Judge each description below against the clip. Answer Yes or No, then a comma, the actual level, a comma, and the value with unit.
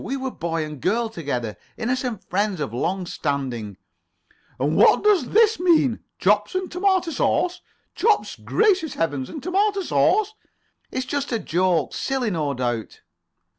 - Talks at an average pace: Yes, average, 145 wpm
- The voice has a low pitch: No, high, 225 Hz